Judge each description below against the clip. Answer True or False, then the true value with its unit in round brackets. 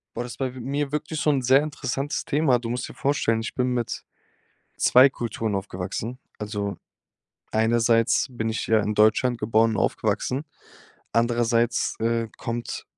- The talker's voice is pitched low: True (120 Hz)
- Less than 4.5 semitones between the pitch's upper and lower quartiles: True (2.7 semitones)